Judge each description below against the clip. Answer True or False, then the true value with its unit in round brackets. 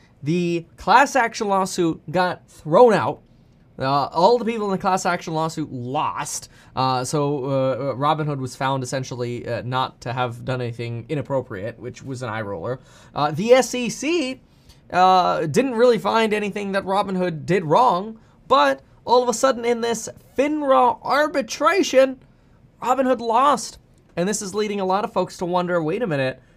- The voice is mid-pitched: True (180 Hz)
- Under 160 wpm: False (170 wpm)